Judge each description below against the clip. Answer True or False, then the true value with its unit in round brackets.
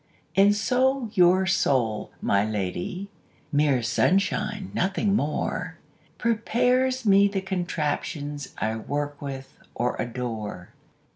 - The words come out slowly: True (100 wpm)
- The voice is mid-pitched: True (175 Hz)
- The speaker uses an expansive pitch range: True (7.9 semitones)